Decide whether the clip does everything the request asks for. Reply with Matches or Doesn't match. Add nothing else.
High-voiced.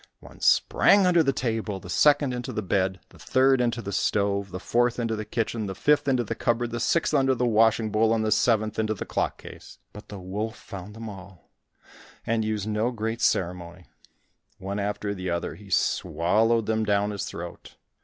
Doesn't match